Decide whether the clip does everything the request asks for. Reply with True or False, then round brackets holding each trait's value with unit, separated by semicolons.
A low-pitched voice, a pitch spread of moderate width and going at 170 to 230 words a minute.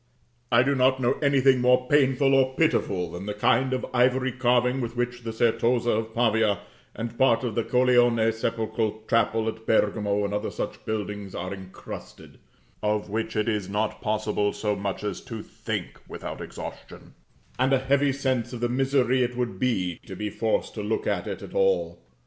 True (120 Hz; 3.2 semitones; 185 wpm)